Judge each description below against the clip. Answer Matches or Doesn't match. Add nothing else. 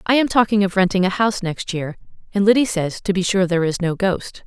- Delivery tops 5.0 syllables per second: Matches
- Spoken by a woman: Matches